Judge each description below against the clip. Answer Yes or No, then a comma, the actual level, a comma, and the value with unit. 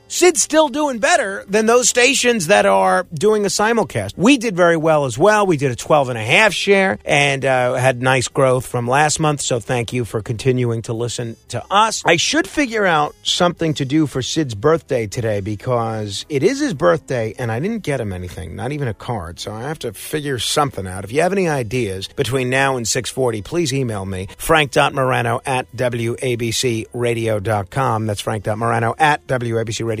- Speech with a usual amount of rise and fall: No, wide, 5.9 semitones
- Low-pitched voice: Yes, low, 130 Hz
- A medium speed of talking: Yes, average, 190 wpm